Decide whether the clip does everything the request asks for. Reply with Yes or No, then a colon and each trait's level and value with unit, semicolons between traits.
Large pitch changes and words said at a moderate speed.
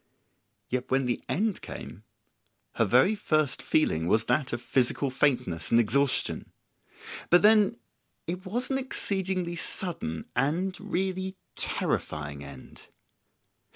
No: wide, 7.7 semitones; slow, 120 wpm